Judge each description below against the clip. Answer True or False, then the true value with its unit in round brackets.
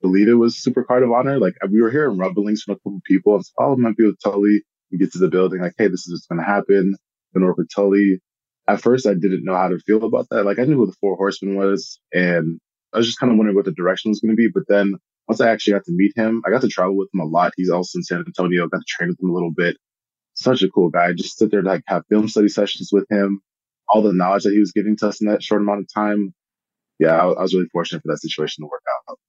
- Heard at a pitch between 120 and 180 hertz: False (100 Hz)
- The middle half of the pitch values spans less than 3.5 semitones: True (2.6 semitones)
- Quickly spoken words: True (295 wpm)